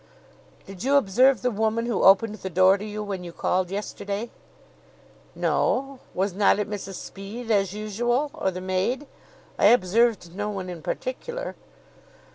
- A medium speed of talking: Yes, average, 155 wpm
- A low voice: No, high, 205 Hz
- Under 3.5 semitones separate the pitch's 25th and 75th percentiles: No, average, 3.8 semitones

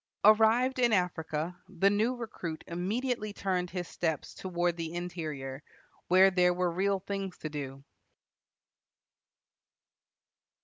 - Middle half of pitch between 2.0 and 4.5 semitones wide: Yes, average, 3.4 semitones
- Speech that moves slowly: Yes, slow, 115 wpm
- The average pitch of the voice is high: No, medium, 180 Hz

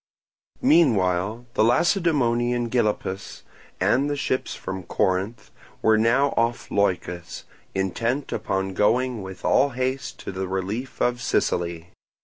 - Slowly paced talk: Yes, slow, 120 wpm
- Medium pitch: No, low, 115 Hz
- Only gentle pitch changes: No, average, 5.1 semitones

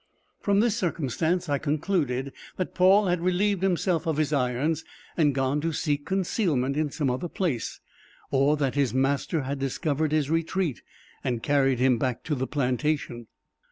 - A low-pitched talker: No, medium, 150 Hz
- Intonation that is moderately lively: Yes, average, 4.4 semitones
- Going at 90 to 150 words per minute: No, average, 160 wpm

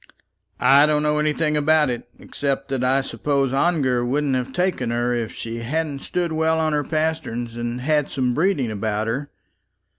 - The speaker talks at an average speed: Yes, average, 175 wpm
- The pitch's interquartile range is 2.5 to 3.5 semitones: No, average, 4.0 semitones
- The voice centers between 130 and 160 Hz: Yes, medium, 140 Hz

